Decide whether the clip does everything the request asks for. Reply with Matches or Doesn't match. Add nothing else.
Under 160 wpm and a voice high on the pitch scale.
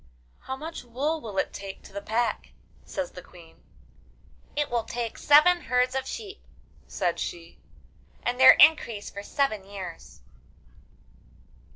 Matches